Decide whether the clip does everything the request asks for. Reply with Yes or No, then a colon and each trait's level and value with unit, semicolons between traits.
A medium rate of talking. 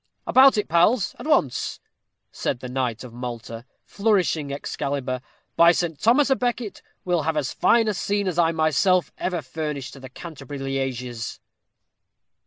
Yes: average, 155 wpm